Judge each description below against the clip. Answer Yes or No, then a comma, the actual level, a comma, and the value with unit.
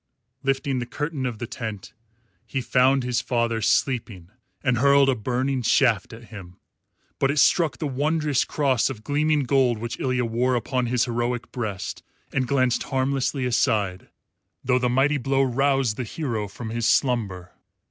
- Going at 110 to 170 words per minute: Yes, average, 160 wpm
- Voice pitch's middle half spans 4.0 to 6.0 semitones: No, average, 2.7 semitones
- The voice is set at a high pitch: No, low, 125 Hz